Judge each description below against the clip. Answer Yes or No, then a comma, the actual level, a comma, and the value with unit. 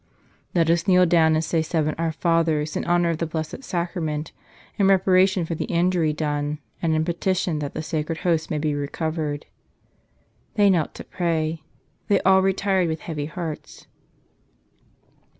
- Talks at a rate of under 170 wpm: Yes, average, 160 wpm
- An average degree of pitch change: No, narrow, 2.2 semitones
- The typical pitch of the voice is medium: Yes, medium, 165 Hz